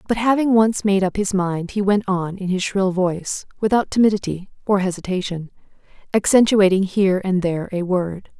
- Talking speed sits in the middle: Yes, average, 165 wpm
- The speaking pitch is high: Yes, high, 195 Hz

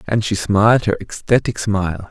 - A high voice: No, low, 105 Hz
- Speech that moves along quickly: No, average, 170 wpm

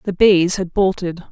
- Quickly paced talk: No, average, 185 wpm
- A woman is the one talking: Yes, female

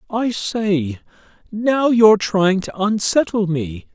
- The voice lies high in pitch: Yes, high, 200 Hz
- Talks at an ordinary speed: No, slow, 120 wpm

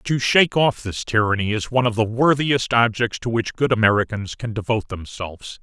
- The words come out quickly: No, average, 190 wpm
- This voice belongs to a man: Yes, male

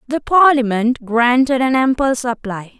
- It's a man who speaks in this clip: No, female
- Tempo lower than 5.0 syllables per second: Yes, 4.4 syllables/s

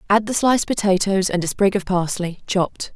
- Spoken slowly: No, fast, 205 wpm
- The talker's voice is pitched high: Yes, high, 195 Hz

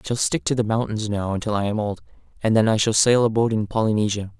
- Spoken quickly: Yes, fast, 275 wpm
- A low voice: Yes, low, 110 Hz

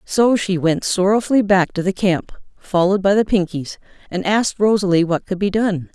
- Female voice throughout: Yes, female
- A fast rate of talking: No, average, 190 wpm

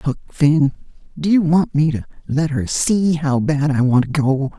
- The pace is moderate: No, fast, 210 wpm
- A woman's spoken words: No, male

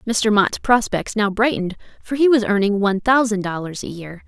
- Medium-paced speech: Yes, average, 195 wpm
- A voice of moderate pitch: No, high, 210 Hz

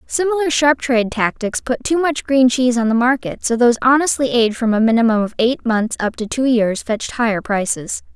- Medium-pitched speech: No, high, 245 Hz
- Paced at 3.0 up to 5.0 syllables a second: No, 5.6 syllables/s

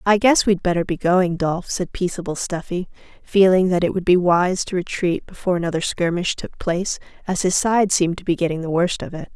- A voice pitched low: No, medium, 180 Hz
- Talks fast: Yes, fast, 220 wpm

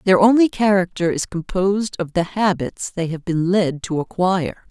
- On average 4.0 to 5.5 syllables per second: Yes, 4.9 syllables/s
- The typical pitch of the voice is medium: Yes, medium, 180 Hz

